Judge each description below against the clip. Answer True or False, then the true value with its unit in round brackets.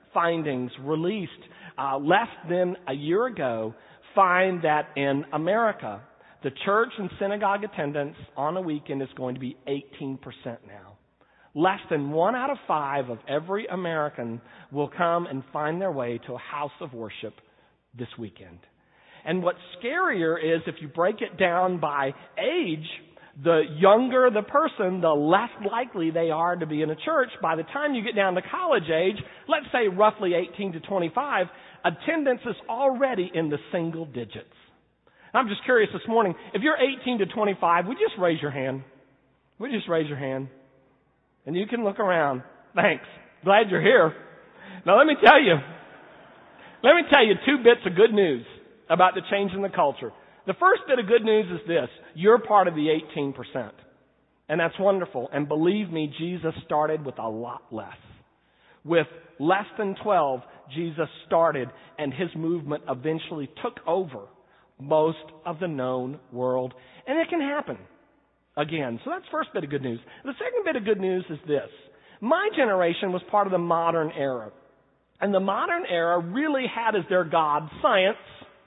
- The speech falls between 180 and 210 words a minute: False (170 wpm)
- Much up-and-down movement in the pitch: True (5.9 semitones)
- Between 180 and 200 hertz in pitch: False (170 Hz)